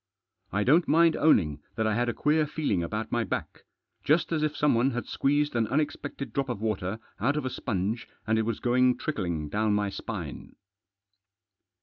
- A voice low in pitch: Yes, low, 120 Hz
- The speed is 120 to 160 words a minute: No, average, 185 wpm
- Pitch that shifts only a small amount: No, wide, 5.5 semitones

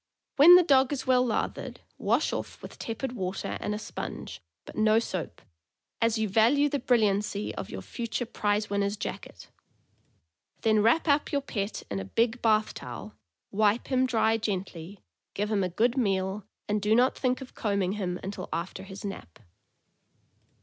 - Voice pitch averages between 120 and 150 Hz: No, high, 215 Hz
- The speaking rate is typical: Yes, average, 170 wpm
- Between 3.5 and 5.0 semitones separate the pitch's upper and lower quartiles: Yes, average, 3.8 semitones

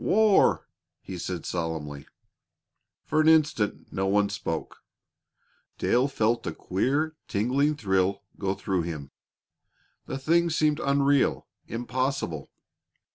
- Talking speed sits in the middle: No, slow, 110 wpm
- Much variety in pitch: Yes, wide, 7.3 semitones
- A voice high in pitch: No, low, 120 Hz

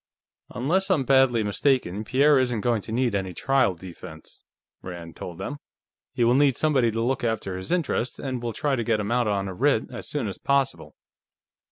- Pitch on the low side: Yes, low, 120 Hz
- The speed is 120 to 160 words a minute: No, average, 195 wpm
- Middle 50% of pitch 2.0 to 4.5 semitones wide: No, average, 4.9 semitones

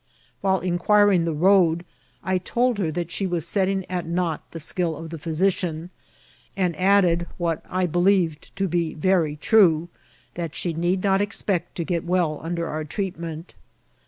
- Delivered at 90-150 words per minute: No, average, 170 wpm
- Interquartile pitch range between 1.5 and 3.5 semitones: Yes, narrow, 2.4 semitones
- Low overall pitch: No, medium, 175 Hz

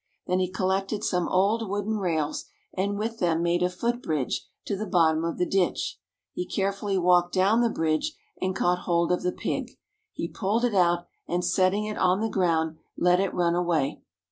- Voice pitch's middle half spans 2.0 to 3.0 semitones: Yes, average, 2.7 semitones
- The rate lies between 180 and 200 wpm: Yes, average, 195 wpm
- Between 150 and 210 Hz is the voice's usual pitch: Yes, medium, 185 Hz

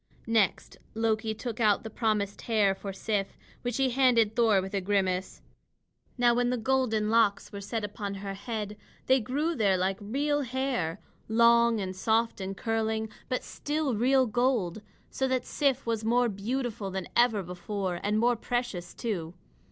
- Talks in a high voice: Yes, high, 220 Hz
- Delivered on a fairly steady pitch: No, average, 3.4 semitones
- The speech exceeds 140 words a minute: Yes, average, 165 wpm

